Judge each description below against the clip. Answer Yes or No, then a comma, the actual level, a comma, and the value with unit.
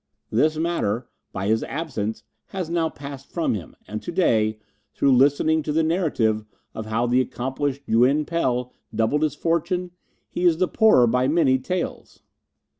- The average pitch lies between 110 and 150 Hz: Yes, medium, 140 Hz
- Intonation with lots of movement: Yes, wide, 5.7 semitones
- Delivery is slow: No, average, 160 wpm